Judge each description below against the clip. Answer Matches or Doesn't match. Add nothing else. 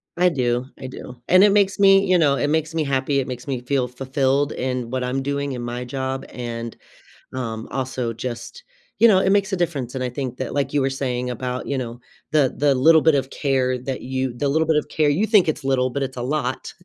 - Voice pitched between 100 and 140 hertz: Matches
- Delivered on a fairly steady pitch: Doesn't match